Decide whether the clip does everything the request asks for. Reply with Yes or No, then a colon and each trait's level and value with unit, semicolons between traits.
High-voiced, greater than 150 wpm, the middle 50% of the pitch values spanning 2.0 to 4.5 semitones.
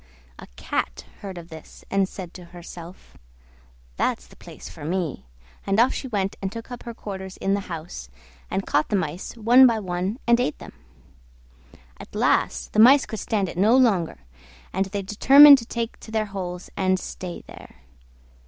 Yes: high, 195 Hz; average, 180 wpm; average, 4.2 semitones